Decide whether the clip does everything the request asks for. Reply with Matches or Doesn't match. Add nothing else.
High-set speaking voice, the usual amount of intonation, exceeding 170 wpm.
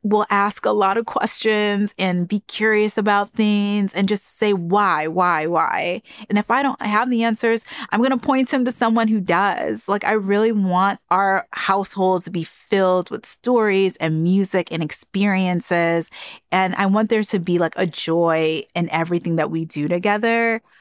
Matches